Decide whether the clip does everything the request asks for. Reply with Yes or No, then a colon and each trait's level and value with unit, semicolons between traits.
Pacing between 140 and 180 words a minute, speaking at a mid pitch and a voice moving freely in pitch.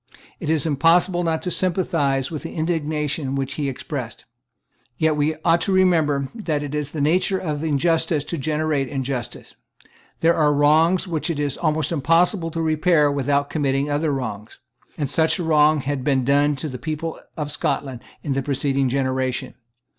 No: average, 170 wpm; medium, 150 Hz; average, 2.8 semitones